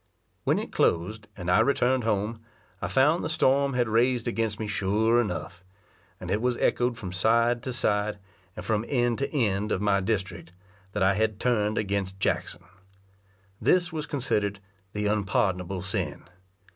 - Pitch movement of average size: Yes, average, 3.8 semitones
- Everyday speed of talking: Yes, average, 160 wpm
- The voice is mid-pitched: No, low, 110 Hz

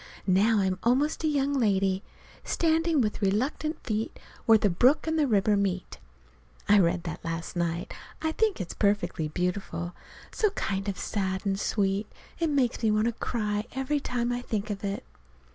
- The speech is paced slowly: No, average, 170 wpm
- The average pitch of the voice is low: No, high, 210 Hz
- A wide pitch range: No, average, 5.0 semitones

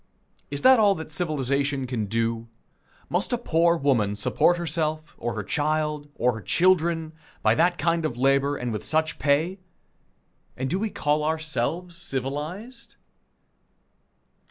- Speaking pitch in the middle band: Yes, medium, 155 Hz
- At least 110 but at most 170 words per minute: Yes, average, 140 wpm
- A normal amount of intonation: Yes, average, 4.1 semitones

